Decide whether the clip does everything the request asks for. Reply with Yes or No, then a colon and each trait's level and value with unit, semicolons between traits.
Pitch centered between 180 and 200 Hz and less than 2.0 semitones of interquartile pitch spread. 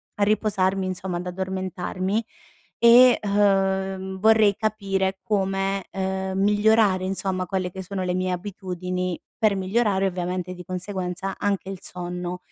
Yes: high, 190 Hz; narrow, 1.5 semitones